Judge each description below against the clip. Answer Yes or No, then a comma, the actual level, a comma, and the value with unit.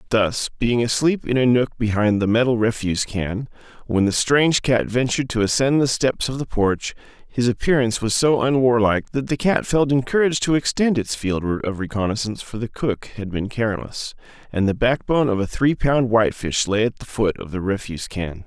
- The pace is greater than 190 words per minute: Yes, average, 200 wpm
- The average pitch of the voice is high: No, low, 120 Hz